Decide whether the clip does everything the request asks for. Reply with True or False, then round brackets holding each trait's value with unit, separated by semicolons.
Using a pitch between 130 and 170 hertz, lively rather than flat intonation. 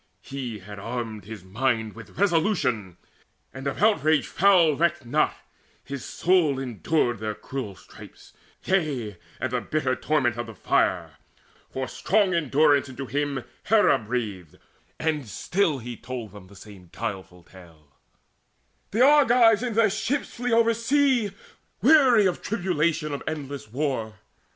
True (140 Hz; 8.9 semitones)